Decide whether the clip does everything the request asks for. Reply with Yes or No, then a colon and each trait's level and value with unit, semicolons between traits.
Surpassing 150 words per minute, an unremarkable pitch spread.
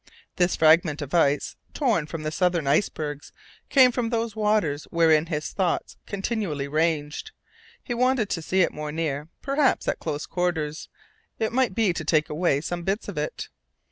No: average, 170 wpm; wide, 5.9 semitones